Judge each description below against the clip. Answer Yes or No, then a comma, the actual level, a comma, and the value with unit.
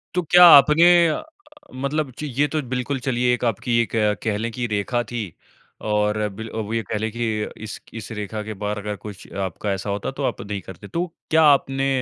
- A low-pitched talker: Yes, low, 115 Hz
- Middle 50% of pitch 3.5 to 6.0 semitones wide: Yes, average, 4.5 semitones